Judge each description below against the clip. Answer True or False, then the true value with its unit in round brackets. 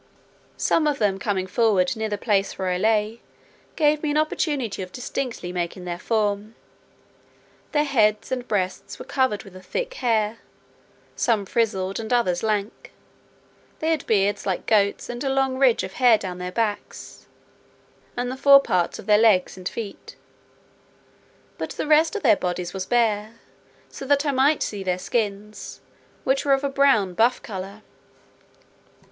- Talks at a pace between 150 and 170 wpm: True (165 wpm)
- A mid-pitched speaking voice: False (220 Hz)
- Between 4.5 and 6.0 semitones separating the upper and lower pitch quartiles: True (5.2 semitones)